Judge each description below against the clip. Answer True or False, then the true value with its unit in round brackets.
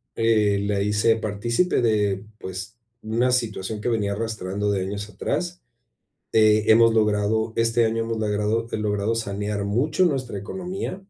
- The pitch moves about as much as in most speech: False (2.0 semitones)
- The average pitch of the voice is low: True (110 Hz)